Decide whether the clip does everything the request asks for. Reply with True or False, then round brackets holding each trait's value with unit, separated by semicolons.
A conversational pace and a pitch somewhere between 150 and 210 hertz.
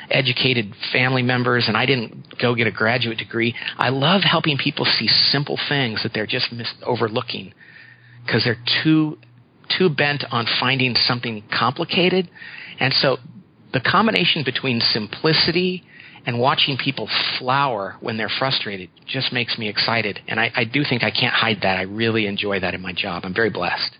False (170 wpm; 120 Hz)